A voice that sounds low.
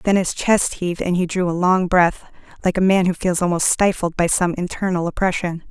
No: medium, 180 Hz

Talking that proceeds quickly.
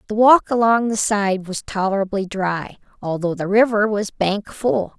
No: average, 170 wpm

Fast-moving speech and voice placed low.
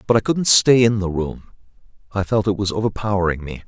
Yes: fast, 215 wpm; low, 100 Hz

